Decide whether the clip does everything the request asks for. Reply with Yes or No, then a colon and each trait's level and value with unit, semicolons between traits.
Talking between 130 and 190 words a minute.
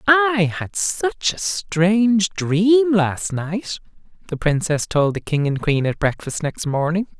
Yes: average, 160 wpm